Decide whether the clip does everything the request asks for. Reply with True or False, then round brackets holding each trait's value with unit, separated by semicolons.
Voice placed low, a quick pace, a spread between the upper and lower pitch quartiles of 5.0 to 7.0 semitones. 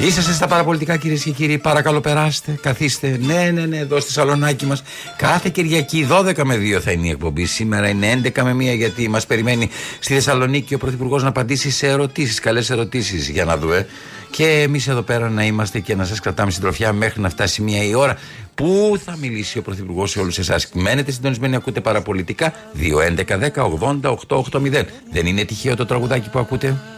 True (130 Hz; 200 wpm; 5.4 semitones)